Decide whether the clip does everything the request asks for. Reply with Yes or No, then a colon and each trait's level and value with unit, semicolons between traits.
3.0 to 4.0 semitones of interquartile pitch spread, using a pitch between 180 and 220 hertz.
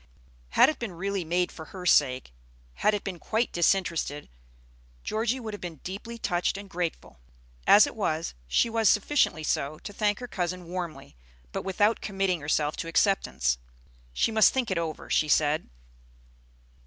No: average, 4.7 semitones; medium, 185 Hz